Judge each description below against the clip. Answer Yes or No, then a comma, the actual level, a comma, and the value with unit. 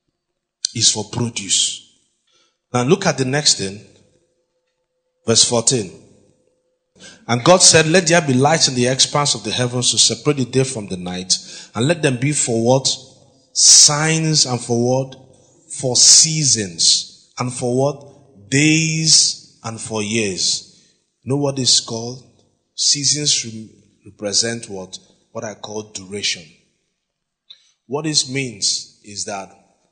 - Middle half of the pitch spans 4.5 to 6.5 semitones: Yes, average, 5.1 semitones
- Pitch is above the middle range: No, low, 130 Hz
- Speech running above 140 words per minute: No, slow, 135 wpm